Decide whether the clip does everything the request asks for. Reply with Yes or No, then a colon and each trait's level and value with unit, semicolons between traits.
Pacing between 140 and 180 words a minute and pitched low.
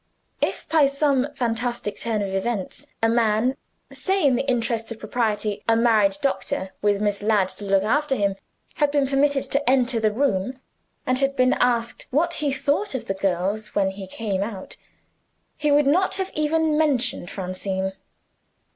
No: average, 170 wpm; high, 235 Hz